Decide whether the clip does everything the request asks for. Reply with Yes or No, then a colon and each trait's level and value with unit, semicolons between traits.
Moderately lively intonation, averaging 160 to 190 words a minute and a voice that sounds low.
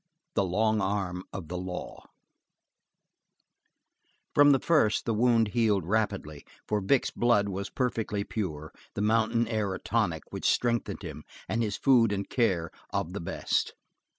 No: average, 3.3 semitones; average, 150 wpm; low, 105 Hz